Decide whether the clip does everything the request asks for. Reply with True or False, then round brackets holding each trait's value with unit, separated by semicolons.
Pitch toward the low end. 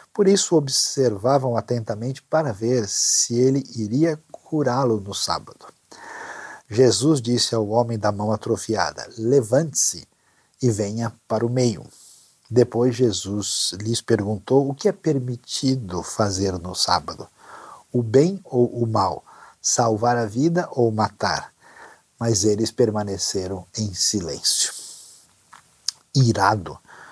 True (120 Hz)